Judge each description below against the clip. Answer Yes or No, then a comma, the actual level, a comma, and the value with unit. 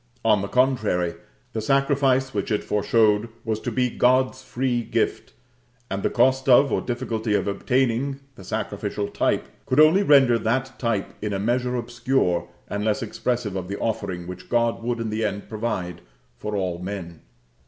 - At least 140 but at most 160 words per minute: No, average, 170 wpm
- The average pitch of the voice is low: Yes, low, 115 Hz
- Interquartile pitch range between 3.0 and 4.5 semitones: Yes, average, 3.9 semitones